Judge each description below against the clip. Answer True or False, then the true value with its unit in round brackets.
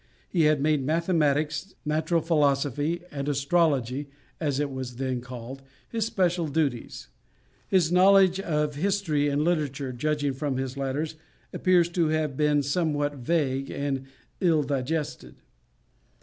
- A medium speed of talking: False (130 wpm)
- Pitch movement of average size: True (3.1 semitones)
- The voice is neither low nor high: True (150 Hz)